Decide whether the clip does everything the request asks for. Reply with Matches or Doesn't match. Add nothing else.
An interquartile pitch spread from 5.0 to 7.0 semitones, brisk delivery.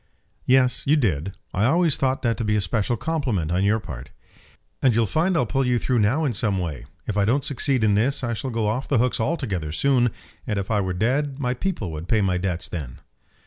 Matches